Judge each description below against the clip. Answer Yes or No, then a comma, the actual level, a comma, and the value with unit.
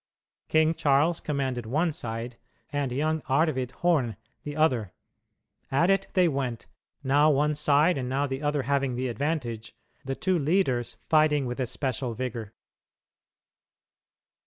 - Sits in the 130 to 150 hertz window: Yes, medium, 140 Hz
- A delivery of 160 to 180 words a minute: No, slow, 135 wpm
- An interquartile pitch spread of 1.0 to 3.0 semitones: No, average, 3.6 semitones